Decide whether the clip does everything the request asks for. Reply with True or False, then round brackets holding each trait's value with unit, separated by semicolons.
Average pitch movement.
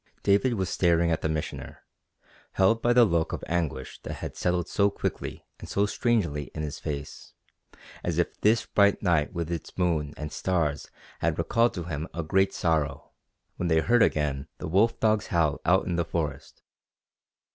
True (4.5 semitones)